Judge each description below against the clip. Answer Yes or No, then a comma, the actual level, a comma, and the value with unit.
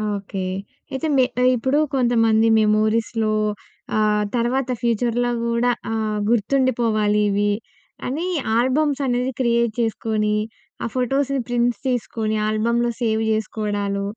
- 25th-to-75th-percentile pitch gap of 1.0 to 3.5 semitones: Yes, narrow, 2.6 semitones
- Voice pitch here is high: Yes, high, 230 Hz